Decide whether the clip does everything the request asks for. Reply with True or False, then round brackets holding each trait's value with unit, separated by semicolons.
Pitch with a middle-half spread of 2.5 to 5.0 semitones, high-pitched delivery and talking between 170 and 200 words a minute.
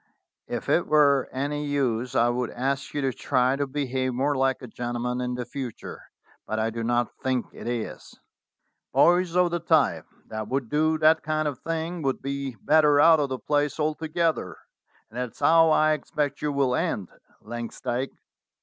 False (3.6 semitones; 140 Hz; 180 wpm)